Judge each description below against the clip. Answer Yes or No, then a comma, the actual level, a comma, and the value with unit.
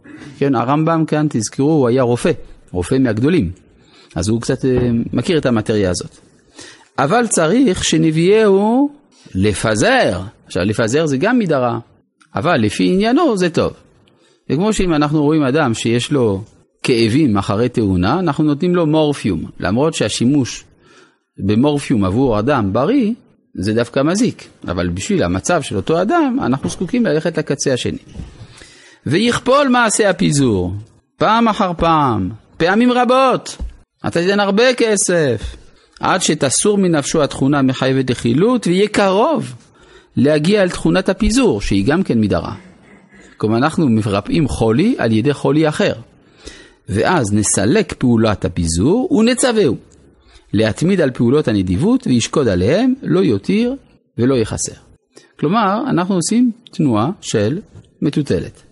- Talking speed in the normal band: Yes, average, 125 wpm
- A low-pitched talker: No, medium, 145 Hz